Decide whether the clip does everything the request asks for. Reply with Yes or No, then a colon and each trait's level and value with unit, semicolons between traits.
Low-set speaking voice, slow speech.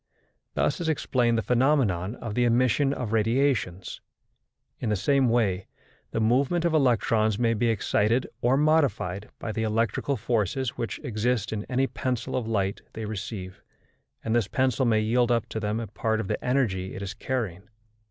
No: low, 115 Hz; average, 170 wpm